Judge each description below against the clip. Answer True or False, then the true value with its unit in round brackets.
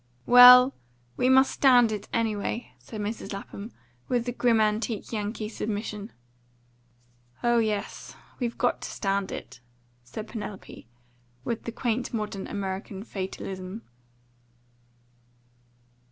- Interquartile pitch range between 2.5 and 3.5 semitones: True (2.8 semitones)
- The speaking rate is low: True (110 wpm)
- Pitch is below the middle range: False (220 Hz)